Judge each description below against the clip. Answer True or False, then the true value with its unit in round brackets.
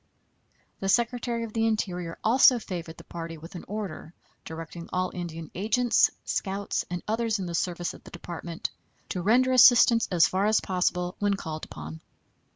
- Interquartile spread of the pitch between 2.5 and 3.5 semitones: False (4.7 semitones)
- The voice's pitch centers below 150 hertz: False (185 Hz)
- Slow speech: False (165 wpm)